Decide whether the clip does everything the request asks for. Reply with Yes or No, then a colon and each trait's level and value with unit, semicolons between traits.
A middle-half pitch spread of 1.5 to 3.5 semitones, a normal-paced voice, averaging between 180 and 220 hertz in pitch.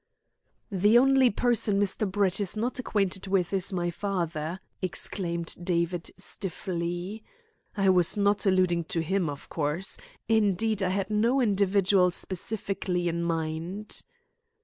No: average, 2.9 semitones; slow, 130 wpm; high, 190 Hz